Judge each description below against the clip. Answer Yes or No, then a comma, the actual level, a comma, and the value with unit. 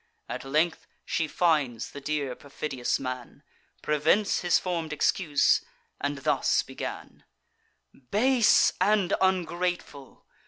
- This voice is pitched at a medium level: Yes, medium, 155 Hz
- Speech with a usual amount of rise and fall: Yes, average, 4.3 semitones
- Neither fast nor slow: No, slow, 105 wpm